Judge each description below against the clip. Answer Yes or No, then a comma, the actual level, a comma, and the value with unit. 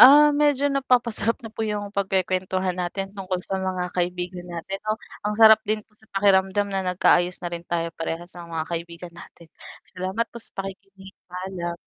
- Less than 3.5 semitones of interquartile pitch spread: Yes, average, 3.0 semitones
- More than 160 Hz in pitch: Yes, high, 190 Hz